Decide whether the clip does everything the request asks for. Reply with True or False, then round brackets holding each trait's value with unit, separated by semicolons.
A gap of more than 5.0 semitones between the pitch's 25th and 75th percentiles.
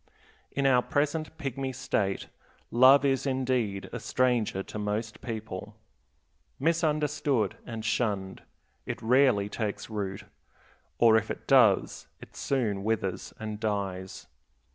False (4.4 semitones)